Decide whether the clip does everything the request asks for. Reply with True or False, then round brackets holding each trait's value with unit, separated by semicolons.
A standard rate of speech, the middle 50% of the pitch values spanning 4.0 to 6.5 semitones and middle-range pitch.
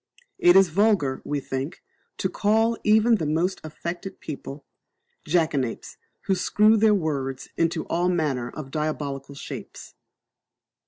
False (125 wpm; 5.5 semitones; 160 Hz)